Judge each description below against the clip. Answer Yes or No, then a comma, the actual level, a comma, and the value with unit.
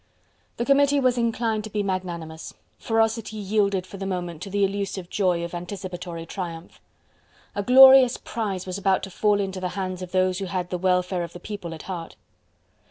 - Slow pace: No, average, 185 wpm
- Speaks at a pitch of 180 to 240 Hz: Yes, high, 190 Hz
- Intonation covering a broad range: No, average, 2.8 semitones